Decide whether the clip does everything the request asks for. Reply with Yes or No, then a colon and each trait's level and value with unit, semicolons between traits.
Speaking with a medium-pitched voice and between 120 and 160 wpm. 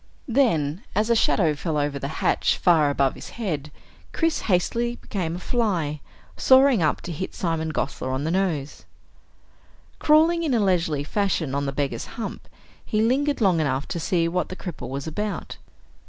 No: medium, 170 Hz; average, 170 wpm